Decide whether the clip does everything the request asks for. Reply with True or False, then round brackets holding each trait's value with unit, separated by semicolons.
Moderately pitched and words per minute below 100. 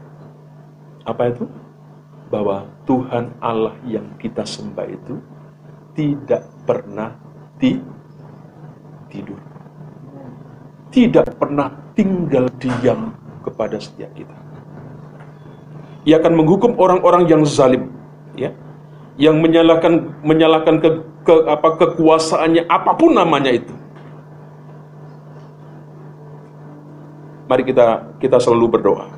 True (150 Hz; 85 wpm)